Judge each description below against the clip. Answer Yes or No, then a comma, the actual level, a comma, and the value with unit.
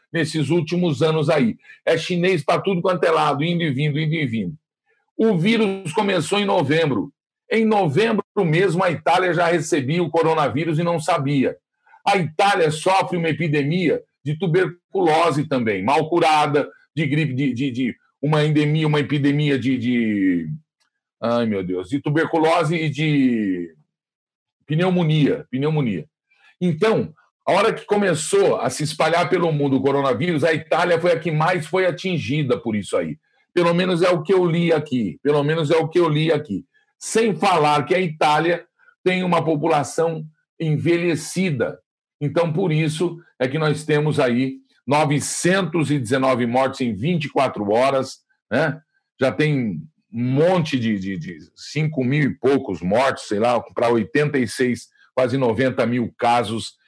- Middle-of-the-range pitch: Yes, medium, 155 Hz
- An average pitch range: Yes, average, 4.0 semitones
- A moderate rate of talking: Yes, average, 155 wpm